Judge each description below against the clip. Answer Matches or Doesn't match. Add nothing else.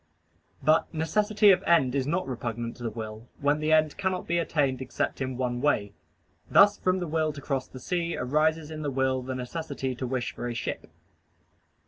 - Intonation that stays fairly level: Doesn't match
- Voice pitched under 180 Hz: Matches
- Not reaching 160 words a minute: Doesn't match